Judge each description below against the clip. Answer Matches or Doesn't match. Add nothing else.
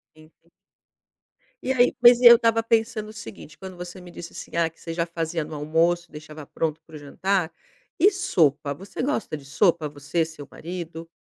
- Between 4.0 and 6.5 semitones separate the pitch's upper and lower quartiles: Matches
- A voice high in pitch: Doesn't match